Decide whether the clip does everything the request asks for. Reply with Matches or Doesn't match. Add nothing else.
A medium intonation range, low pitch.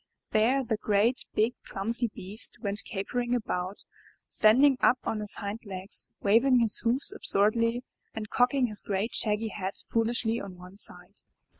Doesn't match